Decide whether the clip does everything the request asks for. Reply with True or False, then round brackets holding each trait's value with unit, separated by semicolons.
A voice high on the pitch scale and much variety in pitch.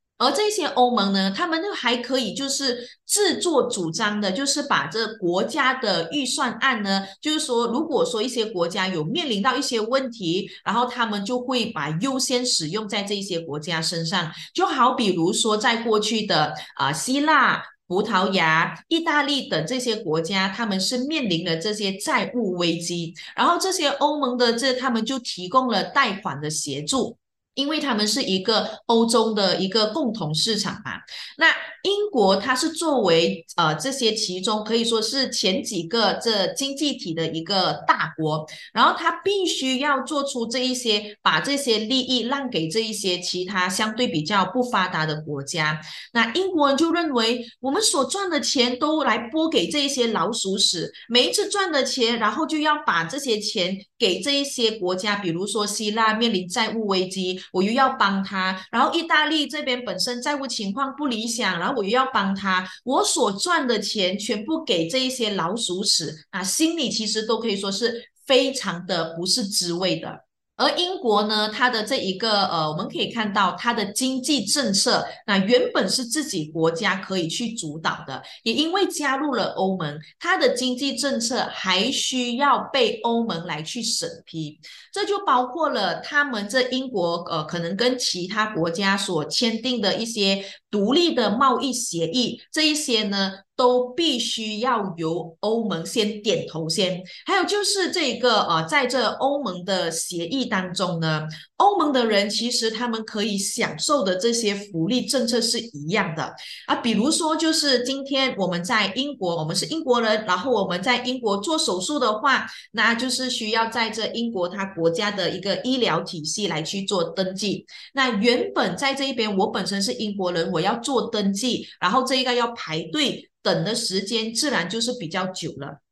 True (225 Hz; 5.9 semitones)